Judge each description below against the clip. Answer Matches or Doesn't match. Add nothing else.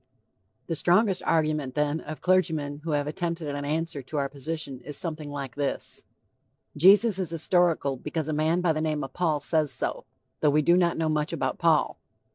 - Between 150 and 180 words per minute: Doesn't match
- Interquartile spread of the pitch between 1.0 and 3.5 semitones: Matches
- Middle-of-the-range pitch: Matches